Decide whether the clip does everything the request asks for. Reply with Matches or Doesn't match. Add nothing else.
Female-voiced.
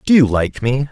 Doesn't match